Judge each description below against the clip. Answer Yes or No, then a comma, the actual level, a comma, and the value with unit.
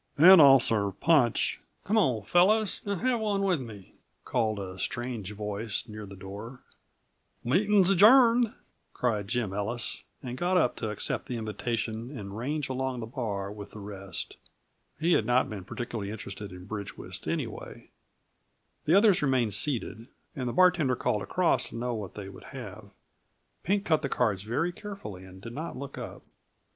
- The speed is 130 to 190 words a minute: Yes, average, 170 wpm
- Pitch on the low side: Yes, low, 120 Hz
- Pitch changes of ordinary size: No, wide, 7.6 semitones